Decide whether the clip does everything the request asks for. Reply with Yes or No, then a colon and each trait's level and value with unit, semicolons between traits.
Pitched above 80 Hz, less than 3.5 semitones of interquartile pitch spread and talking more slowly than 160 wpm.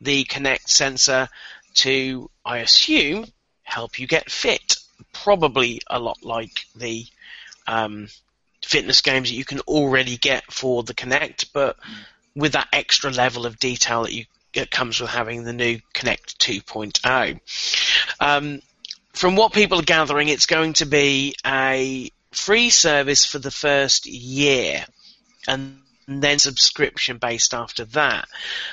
Yes: low, 135 Hz; average, 2.8 semitones; slow, 135 wpm